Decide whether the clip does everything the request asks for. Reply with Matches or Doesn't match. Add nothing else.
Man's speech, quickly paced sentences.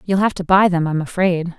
Doesn't match